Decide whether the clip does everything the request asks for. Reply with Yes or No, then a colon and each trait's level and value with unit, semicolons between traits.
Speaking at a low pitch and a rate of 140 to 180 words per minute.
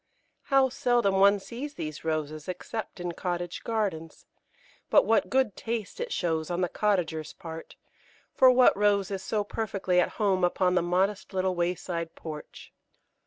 No: medium, 185 Hz; average, 155 wpm